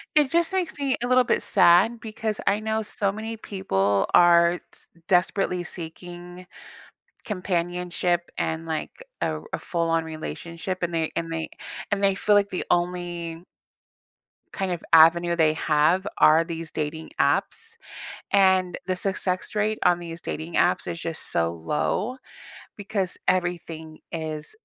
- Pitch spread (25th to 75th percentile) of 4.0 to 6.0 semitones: No, average, 3.3 semitones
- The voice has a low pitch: No, medium, 175 Hz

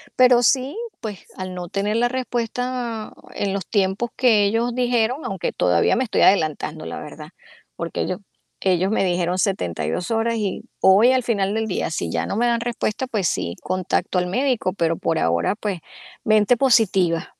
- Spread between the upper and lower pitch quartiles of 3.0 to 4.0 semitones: No, average, 4.9 semitones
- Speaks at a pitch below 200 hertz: No, high, 205 Hz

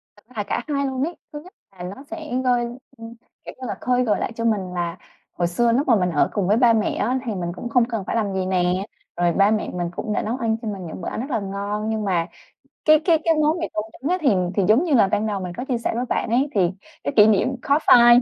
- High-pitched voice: Yes, high, 225 Hz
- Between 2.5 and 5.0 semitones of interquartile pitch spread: Yes, average, 4.4 semitones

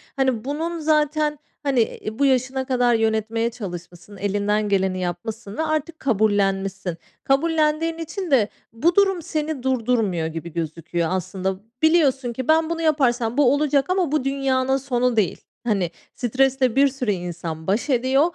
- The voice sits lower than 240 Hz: No, very high, 250 Hz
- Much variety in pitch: Yes, wide, 6.4 semitones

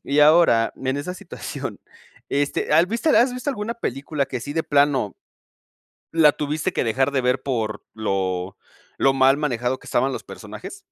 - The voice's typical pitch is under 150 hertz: Yes, medium, 140 Hz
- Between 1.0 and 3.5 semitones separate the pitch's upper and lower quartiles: No, average, 4.2 semitones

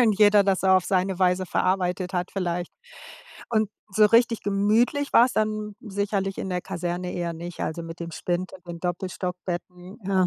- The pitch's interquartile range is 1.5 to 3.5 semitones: Yes, narrow, 2.5 semitones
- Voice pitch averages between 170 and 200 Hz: Yes, medium, 185 Hz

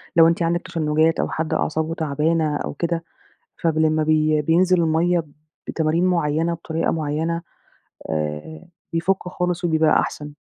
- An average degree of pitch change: No, narrow, 1.5 semitones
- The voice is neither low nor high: Yes, medium, 160 Hz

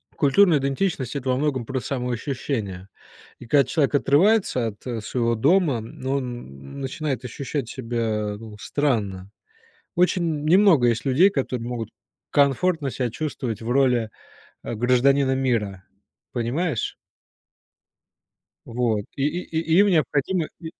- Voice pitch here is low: Yes, low, 130 Hz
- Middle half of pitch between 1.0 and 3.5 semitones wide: No, average, 4.1 semitones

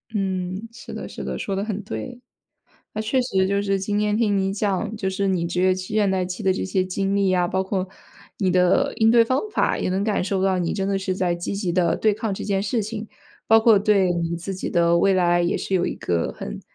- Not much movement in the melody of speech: Yes, narrow, 2.2 semitones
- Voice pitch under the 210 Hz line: Yes, high, 195 Hz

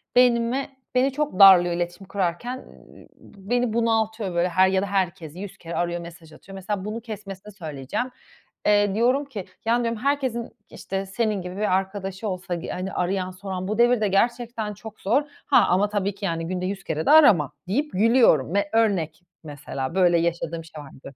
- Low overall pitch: No, high, 195 Hz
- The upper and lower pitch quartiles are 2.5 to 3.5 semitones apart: No, average, 4.3 semitones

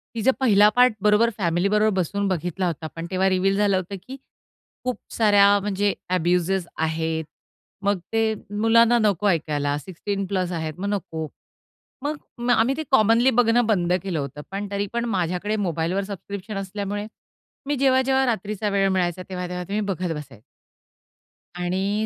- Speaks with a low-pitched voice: No, high, 200 Hz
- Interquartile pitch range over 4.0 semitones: No, average, 3.3 semitones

